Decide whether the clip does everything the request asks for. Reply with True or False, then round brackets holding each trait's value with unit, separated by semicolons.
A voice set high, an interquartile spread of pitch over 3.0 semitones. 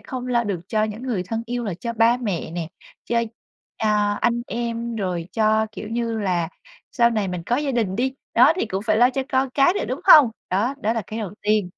False (225 Hz; 2.7 semitones)